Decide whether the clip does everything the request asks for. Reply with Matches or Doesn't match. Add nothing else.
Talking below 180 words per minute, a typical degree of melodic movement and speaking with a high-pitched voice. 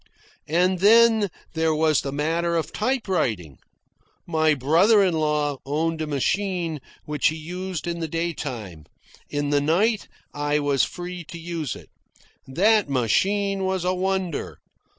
Doesn't match